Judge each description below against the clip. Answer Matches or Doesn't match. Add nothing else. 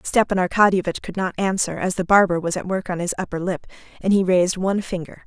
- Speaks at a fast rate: Matches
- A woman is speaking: Matches